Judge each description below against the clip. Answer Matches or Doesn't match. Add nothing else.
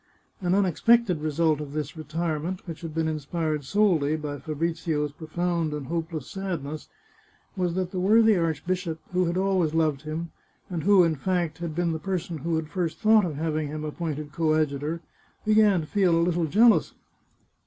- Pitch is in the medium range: Matches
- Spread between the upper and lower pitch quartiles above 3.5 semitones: Doesn't match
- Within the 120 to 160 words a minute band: Doesn't match